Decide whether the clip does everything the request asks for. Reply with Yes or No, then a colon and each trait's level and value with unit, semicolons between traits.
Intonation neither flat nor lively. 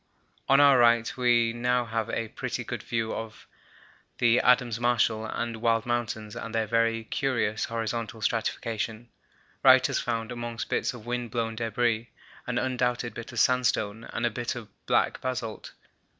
No: narrow, 1.3 semitones